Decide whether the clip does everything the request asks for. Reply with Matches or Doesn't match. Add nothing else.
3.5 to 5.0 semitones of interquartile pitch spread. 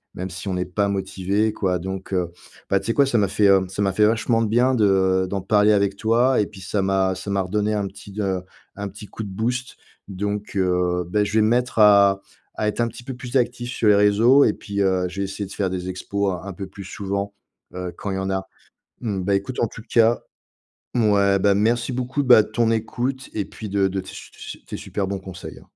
Doesn't match